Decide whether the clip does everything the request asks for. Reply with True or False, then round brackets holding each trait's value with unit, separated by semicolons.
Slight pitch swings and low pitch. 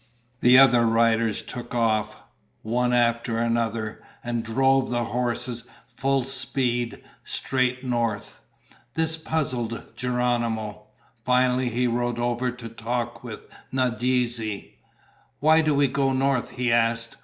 True (1.7 semitones; 120 Hz)